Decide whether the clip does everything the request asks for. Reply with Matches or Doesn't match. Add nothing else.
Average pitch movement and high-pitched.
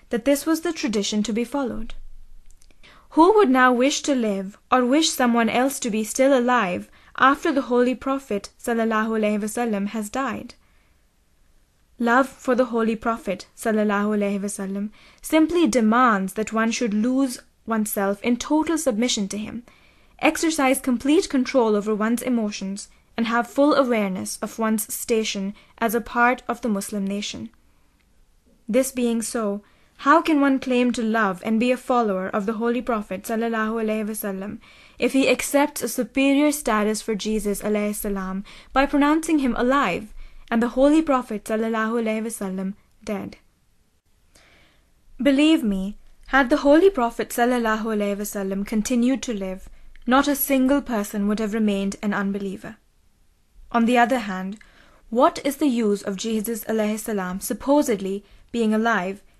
Matches